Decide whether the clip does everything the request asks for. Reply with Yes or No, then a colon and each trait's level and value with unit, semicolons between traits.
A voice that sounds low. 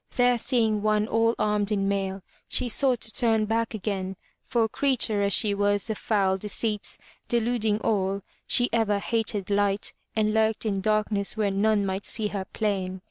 No: high, 210 Hz